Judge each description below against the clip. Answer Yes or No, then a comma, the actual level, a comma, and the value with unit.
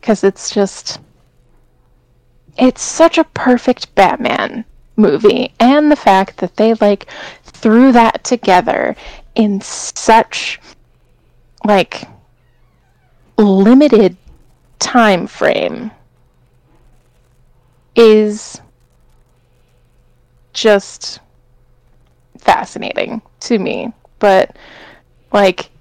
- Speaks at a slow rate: Yes, slow, 70 wpm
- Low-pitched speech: No, high, 195 Hz